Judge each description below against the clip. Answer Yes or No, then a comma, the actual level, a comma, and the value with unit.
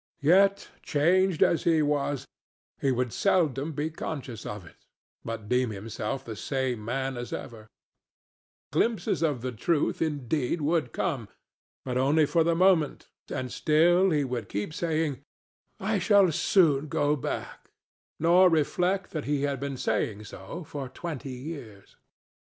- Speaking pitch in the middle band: Yes, medium, 145 Hz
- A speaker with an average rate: Yes, average, 145 wpm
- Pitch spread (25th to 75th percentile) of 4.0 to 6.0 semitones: Yes, average, 4.8 semitones